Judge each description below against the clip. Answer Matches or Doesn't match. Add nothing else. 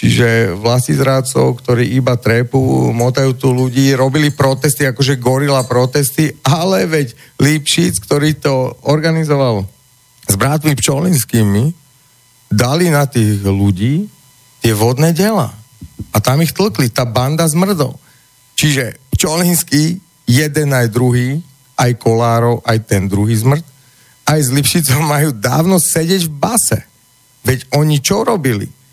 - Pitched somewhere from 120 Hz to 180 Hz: Matches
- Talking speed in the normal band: Matches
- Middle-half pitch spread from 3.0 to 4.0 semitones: Matches